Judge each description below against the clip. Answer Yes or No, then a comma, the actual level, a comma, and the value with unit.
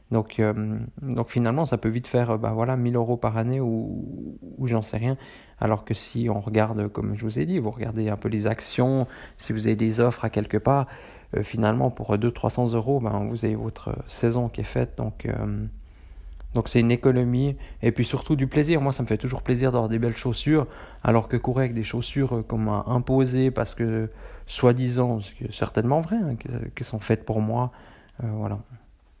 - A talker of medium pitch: No, low, 115 Hz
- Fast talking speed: No, average, 210 wpm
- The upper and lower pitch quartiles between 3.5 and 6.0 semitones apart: No, narrow, 2.5 semitones